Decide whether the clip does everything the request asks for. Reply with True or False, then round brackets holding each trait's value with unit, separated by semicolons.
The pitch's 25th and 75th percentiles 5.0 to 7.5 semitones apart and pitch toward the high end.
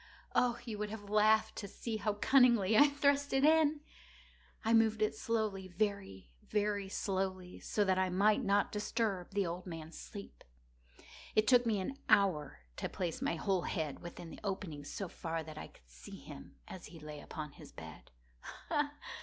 False (3.7 semitones; 200 Hz)